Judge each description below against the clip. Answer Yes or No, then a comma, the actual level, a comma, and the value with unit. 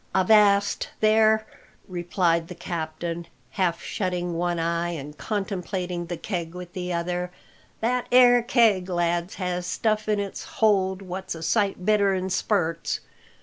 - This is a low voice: No, medium, 180 Hz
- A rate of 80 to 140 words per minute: Yes, slow, 135 wpm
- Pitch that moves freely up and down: No, average, 3.0 semitones